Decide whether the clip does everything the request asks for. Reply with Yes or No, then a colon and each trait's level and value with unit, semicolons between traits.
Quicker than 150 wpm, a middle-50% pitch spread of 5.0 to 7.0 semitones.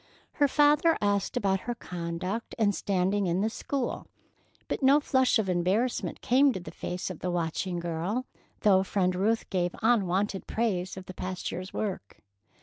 No: average, 165 wpm; average, 4.2 semitones